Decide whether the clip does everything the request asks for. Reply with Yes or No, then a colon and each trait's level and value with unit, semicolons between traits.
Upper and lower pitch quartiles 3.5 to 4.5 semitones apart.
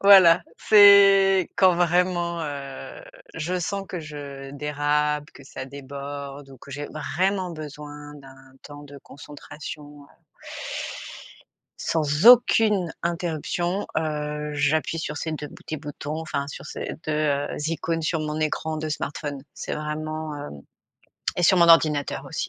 No: average, 2.8 semitones